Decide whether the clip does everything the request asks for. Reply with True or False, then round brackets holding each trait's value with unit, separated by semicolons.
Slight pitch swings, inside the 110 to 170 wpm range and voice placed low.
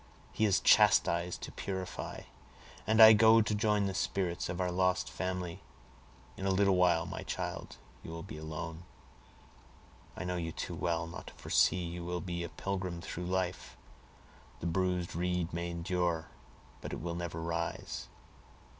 True (1.7 semitones; 165 wpm; 90 Hz)